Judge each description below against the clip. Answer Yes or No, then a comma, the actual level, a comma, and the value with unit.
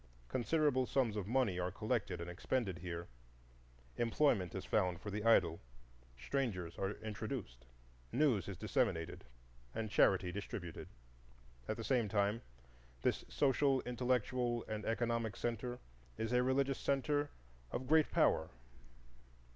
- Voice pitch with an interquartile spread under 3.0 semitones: No, average, 5.1 semitones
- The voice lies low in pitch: Yes, low, 115 Hz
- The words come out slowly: Yes, slow, 125 wpm